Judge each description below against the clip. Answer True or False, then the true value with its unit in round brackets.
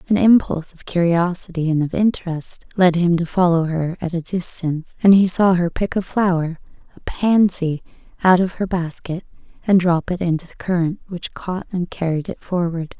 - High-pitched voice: False (175 Hz)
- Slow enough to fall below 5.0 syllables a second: False (5.1 syllables/s)